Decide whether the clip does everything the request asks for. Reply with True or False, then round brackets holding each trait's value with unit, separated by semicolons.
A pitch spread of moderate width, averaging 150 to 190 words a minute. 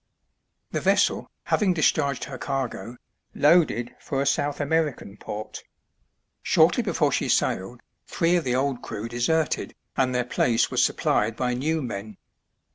False (3.9 semitones; 140 wpm)